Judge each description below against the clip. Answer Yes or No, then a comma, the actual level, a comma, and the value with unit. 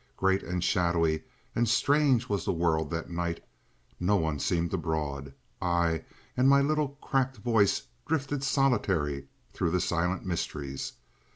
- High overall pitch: No, very low, 90 Hz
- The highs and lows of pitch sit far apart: Yes, wide, 7.3 semitones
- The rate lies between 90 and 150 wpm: Yes, slow, 135 wpm